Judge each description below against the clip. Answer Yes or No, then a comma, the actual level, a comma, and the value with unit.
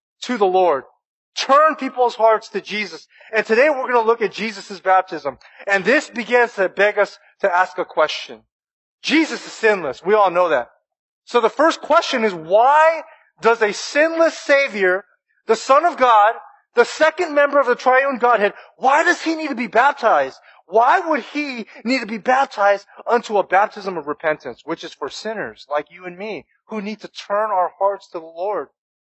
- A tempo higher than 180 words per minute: Yes, average, 190 wpm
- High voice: Yes, high, 225 Hz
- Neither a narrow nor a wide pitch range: No, wide, 6.0 semitones